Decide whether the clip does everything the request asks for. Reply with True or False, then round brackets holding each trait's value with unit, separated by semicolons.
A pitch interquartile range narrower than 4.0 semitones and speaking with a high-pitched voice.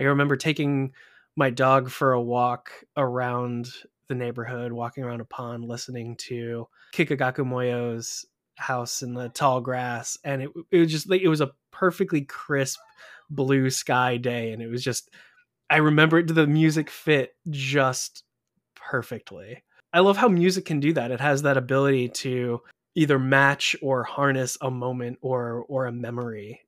False (3.2 semitones; 130 Hz)